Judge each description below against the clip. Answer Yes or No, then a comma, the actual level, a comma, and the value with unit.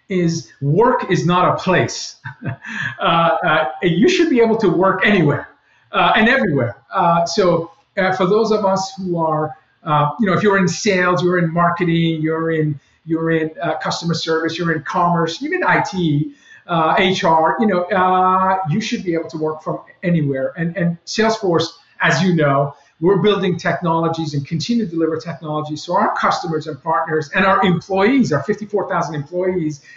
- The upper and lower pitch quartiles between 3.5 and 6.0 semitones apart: No, average, 2.8 semitones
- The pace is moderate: No, fast, 175 wpm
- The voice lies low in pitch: No, medium, 170 Hz